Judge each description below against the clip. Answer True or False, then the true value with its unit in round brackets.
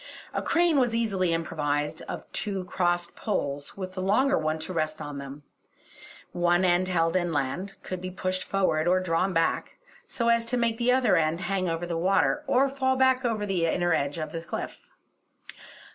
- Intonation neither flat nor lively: True (4.7 semitones)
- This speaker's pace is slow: False (185 wpm)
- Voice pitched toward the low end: False (185 Hz)